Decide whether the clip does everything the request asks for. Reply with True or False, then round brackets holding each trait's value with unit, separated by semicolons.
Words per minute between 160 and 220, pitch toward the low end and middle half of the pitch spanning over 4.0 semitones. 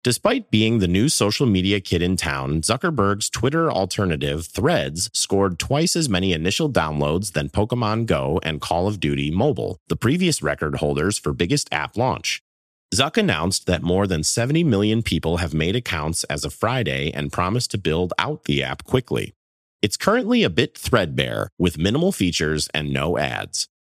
True (170 wpm; 90 Hz; 5.6 semitones)